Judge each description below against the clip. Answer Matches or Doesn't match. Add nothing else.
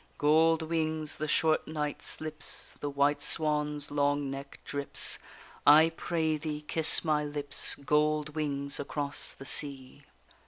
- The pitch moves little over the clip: Matches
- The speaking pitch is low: Doesn't match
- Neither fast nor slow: Doesn't match